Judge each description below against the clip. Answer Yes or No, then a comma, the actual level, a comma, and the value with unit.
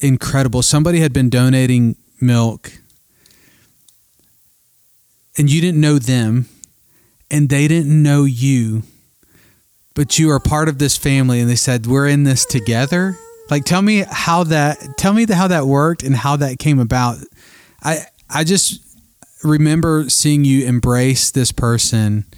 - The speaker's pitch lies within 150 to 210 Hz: No, medium, 140 Hz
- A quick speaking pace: No, average, 145 wpm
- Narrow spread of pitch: No, average, 3.4 semitones